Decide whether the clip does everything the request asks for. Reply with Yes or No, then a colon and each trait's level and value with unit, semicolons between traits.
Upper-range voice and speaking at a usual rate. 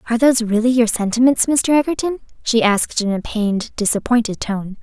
Yes: high, 230 Hz; average, 175 wpm